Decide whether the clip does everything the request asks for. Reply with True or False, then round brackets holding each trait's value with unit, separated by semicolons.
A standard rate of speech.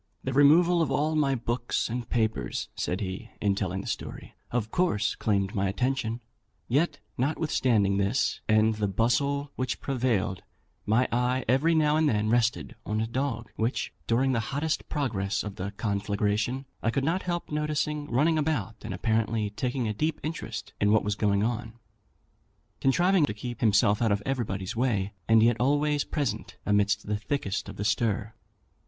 True (165 wpm)